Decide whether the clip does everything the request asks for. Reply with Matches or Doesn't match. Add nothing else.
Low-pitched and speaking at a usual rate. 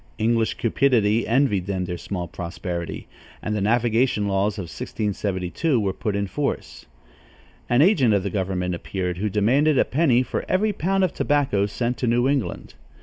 Matches